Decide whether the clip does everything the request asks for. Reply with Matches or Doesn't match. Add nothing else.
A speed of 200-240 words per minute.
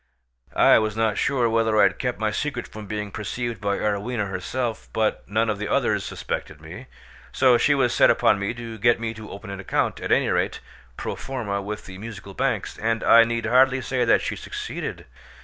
Matches